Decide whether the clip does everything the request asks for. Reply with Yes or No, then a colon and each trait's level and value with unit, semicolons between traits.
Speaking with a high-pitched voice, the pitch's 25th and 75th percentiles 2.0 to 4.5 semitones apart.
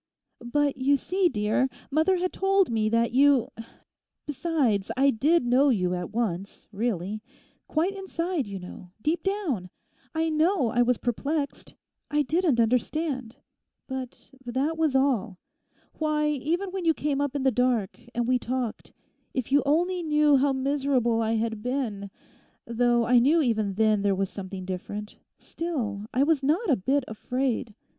No: very high, 260 Hz; average, 5.3 semitones